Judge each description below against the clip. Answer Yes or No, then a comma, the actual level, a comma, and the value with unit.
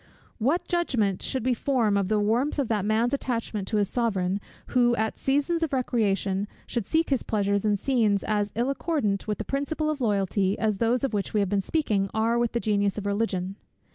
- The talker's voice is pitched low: No, high, 220 Hz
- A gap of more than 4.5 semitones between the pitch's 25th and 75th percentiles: No, average, 4.2 semitones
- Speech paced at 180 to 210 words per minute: Yes, fast, 205 wpm